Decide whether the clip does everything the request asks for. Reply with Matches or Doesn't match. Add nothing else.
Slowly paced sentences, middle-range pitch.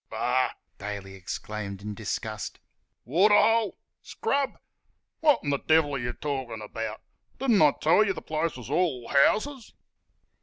Matches